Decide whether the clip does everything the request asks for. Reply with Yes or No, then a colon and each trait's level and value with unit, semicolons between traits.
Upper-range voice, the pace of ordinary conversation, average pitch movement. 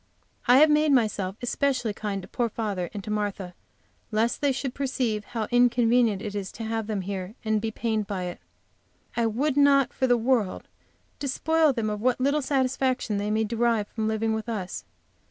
Yes: high, 225 Hz; average, 190 wpm; average, 3.5 semitones